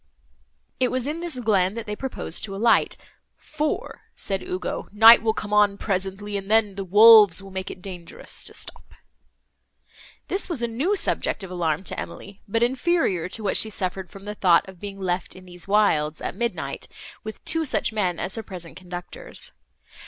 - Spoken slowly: No, average, 185 wpm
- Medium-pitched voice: No, high, 200 Hz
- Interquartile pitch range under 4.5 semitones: Yes, average, 3.6 semitones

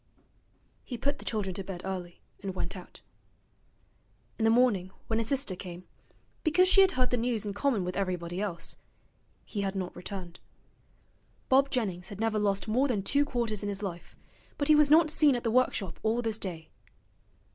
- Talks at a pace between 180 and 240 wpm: Yes, average, 190 wpm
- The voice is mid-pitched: No, high, 215 Hz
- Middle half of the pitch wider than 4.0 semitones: Yes, average, 5.2 semitones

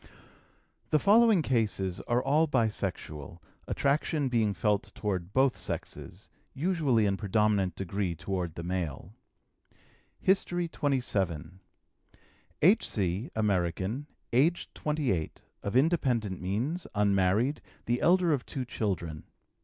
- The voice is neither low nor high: No, low, 110 Hz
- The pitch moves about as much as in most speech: No, wide, 7.3 semitones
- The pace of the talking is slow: Yes, slow, 105 wpm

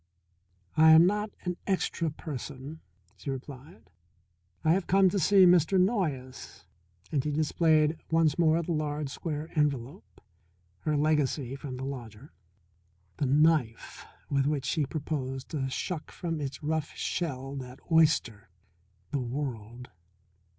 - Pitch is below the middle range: No, medium, 150 Hz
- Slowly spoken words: Yes, slow, 130 wpm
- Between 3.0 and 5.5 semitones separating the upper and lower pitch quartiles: Yes, average, 3.4 semitones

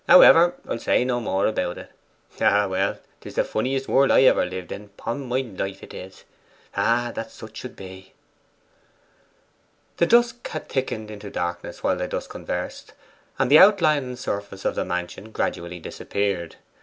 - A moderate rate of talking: Yes, average, 160 wpm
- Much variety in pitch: Yes, wide, 5.7 semitones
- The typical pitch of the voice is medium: No, low, 110 Hz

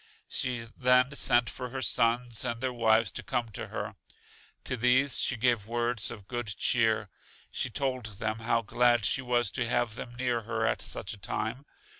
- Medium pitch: No, low, 120 Hz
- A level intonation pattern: Yes, narrow, 1.9 semitones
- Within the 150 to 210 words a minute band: Yes, average, 185 wpm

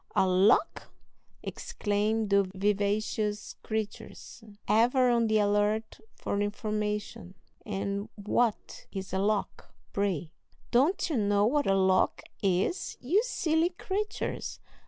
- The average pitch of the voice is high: Yes, high, 210 Hz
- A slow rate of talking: Yes, slow, 115 wpm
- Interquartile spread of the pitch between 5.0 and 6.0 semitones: No, average, 2.8 semitones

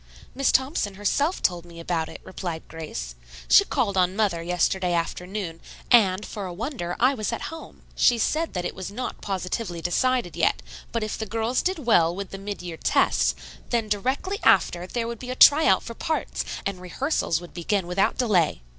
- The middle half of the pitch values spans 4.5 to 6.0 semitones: Yes, wide, 5.5 semitones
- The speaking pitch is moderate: No, high, 195 Hz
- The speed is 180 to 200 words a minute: Yes, average, 190 wpm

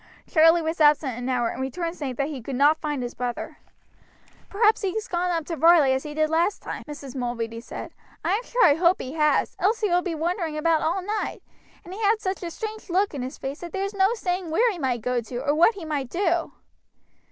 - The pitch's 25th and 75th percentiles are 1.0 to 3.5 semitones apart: No, average, 5.3 semitones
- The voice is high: Yes, very high, 325 Hz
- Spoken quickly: Yes, fast, 235 wpm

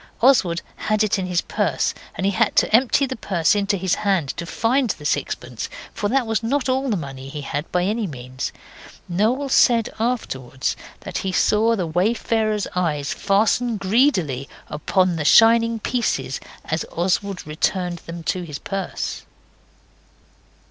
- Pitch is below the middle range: No, high, 195 Hz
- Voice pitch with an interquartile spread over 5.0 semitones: Yes, wide, 5.4 semitones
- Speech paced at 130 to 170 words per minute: Yes, average, 155 wpm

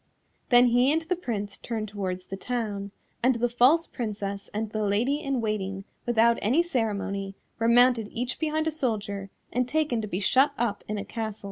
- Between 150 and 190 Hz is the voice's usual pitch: No, high, 230 Hz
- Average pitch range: Yes, average, 3.8 semitones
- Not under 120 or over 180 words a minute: No, average, 190 wpm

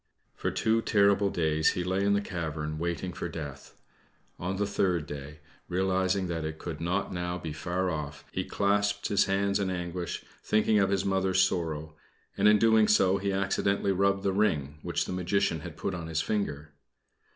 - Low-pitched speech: Yes, very low, 95 Hz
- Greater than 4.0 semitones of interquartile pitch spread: No, average, 3.4 semitones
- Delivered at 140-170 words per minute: No, average, 185 wpm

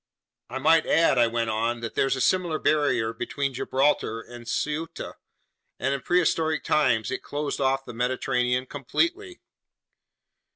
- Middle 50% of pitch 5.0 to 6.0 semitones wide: No, average, 4.1 semitones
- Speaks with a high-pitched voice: No, low, 135 Hz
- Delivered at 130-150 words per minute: Yes, average, 140 wpm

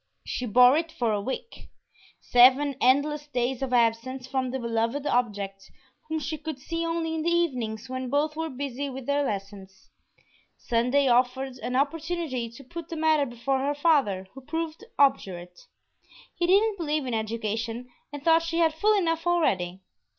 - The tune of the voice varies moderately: Yes, average, 5.0 semitones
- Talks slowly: No, average, 165 wpm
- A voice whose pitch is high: Yes, very high, 270 Hz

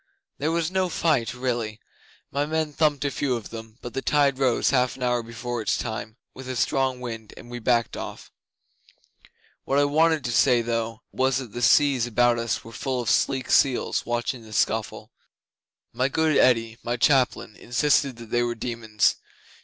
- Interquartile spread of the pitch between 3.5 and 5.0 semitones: No, average, 2.9 semitones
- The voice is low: Yes, low, 125 Hz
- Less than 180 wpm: No, average, 185 wpm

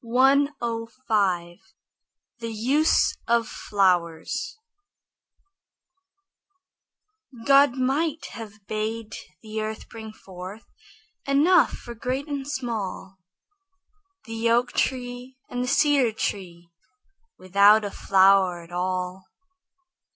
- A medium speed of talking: No, slow, 85 wpm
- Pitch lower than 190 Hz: No, high, 225 Hz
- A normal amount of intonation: Yes, average, 4.9 semitones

